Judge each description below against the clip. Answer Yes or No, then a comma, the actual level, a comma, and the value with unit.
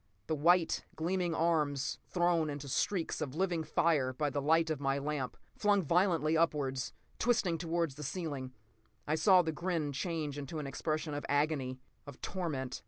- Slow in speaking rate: No, average, 165 wpm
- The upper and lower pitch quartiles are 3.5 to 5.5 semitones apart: No, average, 3.1 semitones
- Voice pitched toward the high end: No, medium, 155 Hz